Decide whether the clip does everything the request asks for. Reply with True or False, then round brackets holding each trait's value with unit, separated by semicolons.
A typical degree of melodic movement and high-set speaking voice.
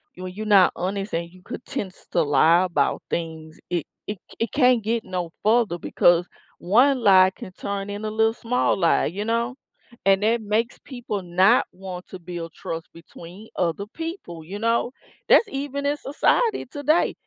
True (4.8 semitones; 200 Hz)